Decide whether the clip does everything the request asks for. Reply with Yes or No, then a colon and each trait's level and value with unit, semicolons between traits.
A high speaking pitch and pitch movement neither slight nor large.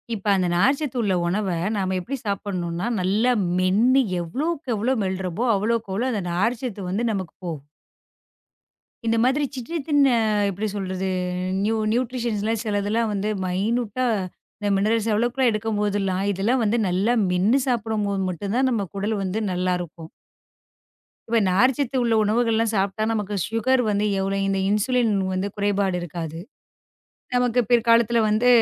Yes: high, 210 Hz; average, 3.6 semitones